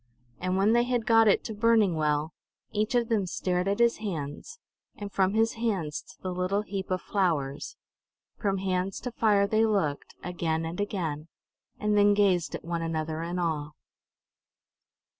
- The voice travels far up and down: No, average, 4.3 semitones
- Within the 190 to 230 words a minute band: No, average, 170 wpm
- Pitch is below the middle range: No, high, 190 Hz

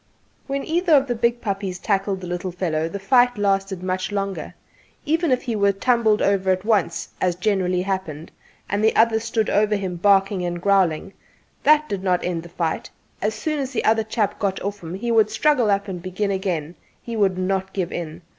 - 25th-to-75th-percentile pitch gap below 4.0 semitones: Yes, average, 3.2 semitones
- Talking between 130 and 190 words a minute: No, fast, 205 wpm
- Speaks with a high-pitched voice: Yes, high, 200 Hz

